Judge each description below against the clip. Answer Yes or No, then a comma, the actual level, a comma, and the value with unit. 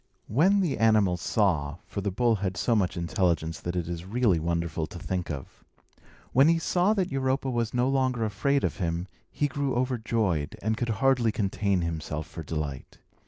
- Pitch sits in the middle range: No, low, 105 Hz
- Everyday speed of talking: Yes, average, 180 wpm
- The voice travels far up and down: Yes, wide, 6.9 semitones